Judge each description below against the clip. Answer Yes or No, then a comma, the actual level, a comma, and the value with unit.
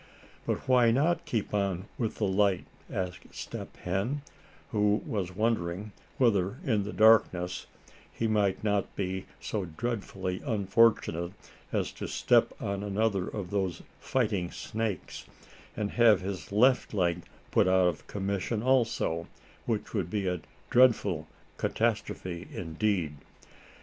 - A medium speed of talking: No, slow, 130 wpm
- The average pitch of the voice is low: Yes, low, 100 Hz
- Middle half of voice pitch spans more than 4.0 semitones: No, average, 3.6 semitones